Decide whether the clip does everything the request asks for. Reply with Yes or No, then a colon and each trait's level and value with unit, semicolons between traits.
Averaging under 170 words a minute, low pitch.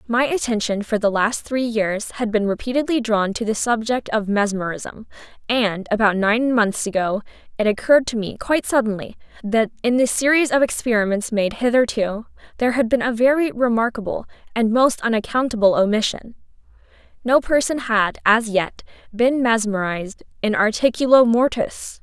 No: average, 145 wpm; high, 225 Hz